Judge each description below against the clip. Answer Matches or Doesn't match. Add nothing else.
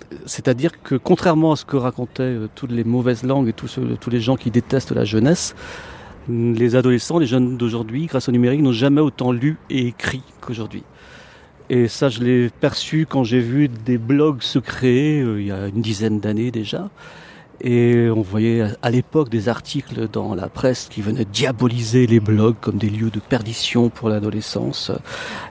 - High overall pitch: Doesn't match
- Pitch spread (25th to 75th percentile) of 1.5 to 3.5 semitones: Matches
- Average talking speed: Matches